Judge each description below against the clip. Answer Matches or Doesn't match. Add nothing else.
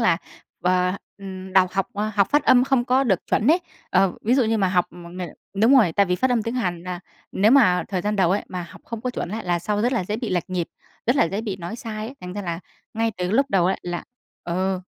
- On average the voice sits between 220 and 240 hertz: Doesn't match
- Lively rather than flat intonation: Doesn't match